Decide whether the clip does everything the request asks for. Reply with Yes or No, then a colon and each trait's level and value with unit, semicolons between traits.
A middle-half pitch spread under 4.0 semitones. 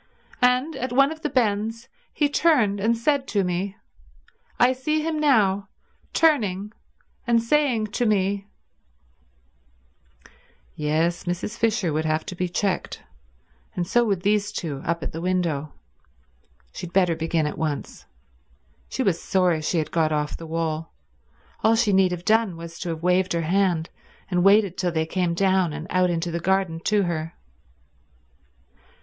No: average, 4.9 semitones